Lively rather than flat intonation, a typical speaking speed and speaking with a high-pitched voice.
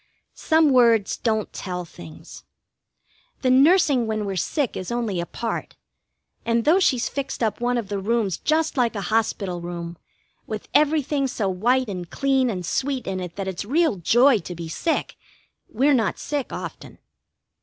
Yes: wide, 6.0 semitones; average, 165 wpm; high, 230 Hz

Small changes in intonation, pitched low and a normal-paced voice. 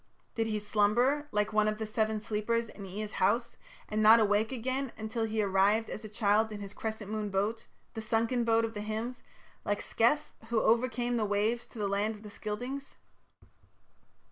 No: narrow, 1.7 semitones; high, 220 Hz; average, 195 wpm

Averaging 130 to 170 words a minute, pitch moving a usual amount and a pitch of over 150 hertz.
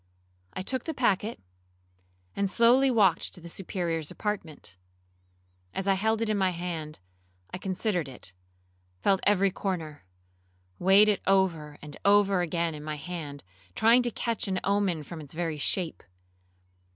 Yes: average, 150 wpm; average, 4.0 semitones; medium, 185 Hz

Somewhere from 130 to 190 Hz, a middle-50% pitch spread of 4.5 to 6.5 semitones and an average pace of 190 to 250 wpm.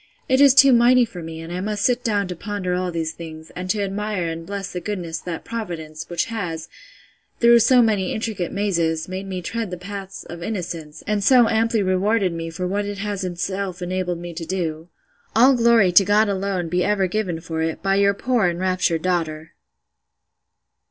No: medium, 185 Hz; average, 3.5 semitones; average, 200 wpm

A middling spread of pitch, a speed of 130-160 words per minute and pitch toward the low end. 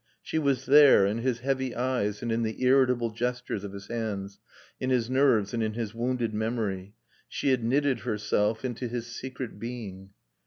No: average, 3.1 semitones; average, 180 wpm; low, 120 Hz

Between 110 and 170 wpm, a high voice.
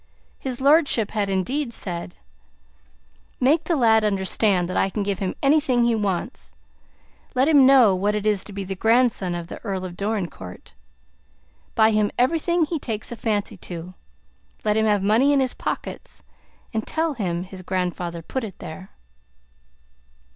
Yes: average, 160 wpm; high, 210 Hz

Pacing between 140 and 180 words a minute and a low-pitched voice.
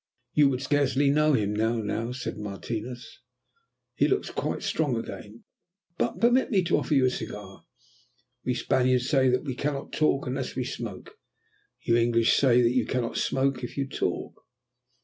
Yes: average, 160 wpm; low, 125 Hz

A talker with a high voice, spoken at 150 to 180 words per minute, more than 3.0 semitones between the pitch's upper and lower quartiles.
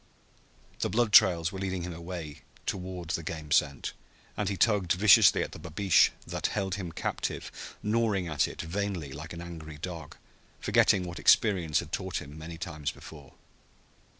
No: very low, 85 Hz; average, 165 wpm; average, 3.4 semitones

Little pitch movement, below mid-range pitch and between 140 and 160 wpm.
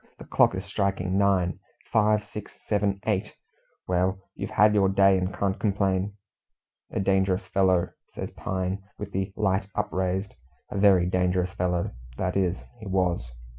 Yes: narrow, 1.5 semitones; very low, 95 Hz; average, 150 wpm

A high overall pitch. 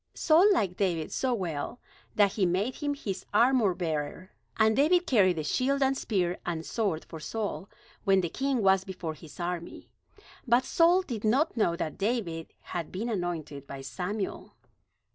Yes: high, 195 Hz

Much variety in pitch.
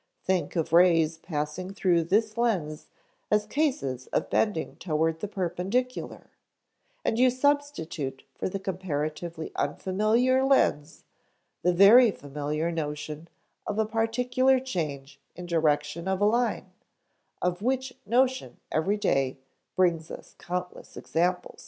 Yes: wide, 6.0 semitones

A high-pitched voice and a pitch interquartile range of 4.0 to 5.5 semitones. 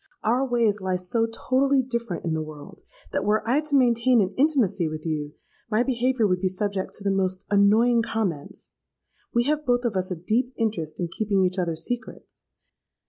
Yes: high, 215 Hz; average, 4.9 semitones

